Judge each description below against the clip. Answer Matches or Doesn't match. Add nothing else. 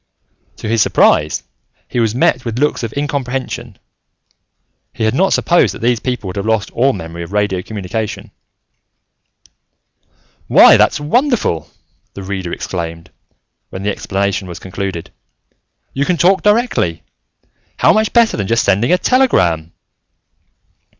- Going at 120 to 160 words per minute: Matches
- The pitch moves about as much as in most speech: Doesn't match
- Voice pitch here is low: Matches